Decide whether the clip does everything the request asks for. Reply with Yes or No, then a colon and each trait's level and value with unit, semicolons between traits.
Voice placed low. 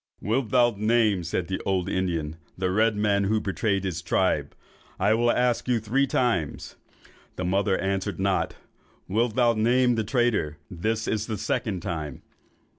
Yes: low, 105 Hz